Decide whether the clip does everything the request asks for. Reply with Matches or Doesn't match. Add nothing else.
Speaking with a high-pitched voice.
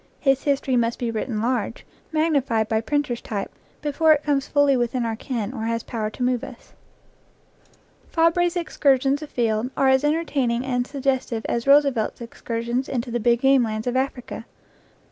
Matches